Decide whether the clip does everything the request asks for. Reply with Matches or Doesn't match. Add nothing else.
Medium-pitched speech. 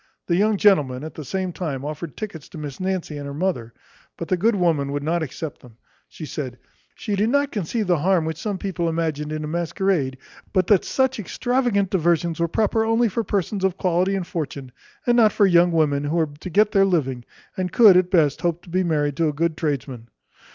Matches